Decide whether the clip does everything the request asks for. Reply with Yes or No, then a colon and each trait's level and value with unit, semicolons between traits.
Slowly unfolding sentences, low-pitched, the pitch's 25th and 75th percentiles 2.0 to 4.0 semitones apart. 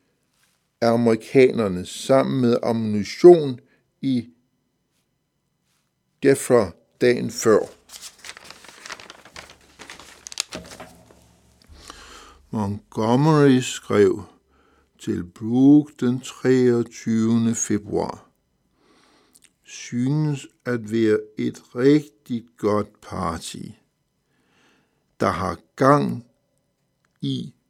Yes: slow, 60 wpm; low, 120 Hz; average, 3.3 semitones